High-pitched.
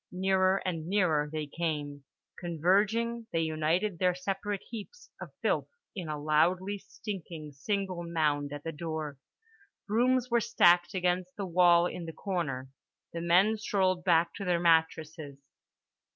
No: medium, 175 Hz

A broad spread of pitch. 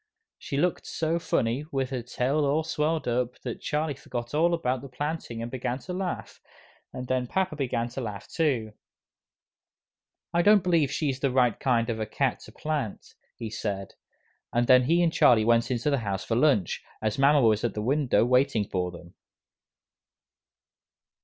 No: average, 4.5 semitones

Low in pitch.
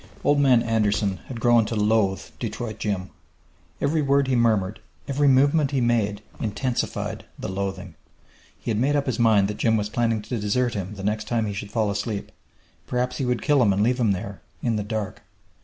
Yes: low, 110 Hz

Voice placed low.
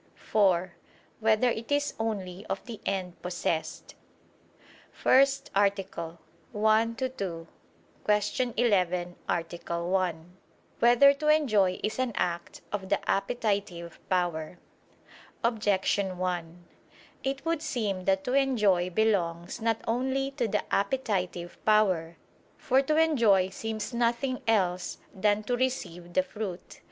No: high, 205 Hz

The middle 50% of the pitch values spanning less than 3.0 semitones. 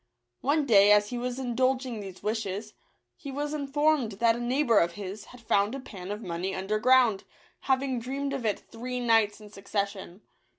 No: average, 4.2 semitones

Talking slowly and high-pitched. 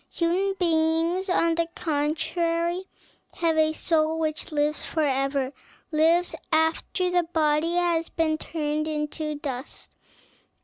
Yes: slow, 115 wpm; very high, 320 Hz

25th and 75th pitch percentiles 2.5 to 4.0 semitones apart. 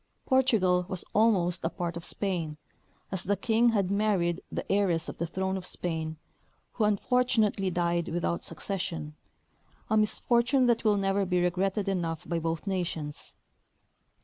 Yes: average, 3.5 semitones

